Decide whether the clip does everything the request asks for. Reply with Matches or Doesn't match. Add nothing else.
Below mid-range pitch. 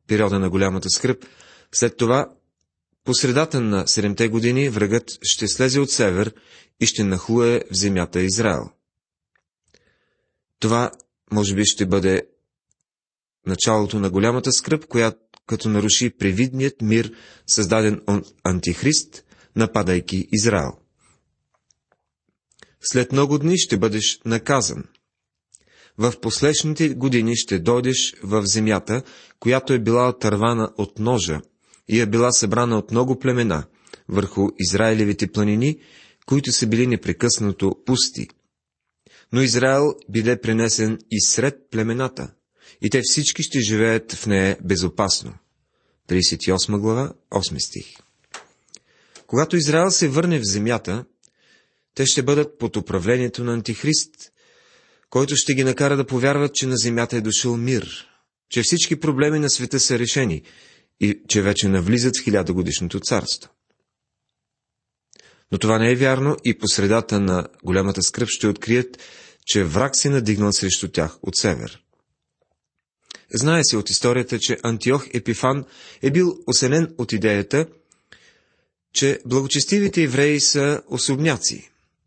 Matches